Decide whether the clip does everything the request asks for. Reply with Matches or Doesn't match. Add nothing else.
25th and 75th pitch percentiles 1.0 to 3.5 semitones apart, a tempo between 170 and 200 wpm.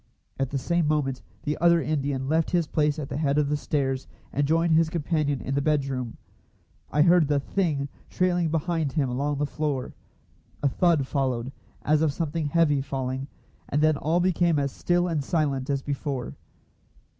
Matches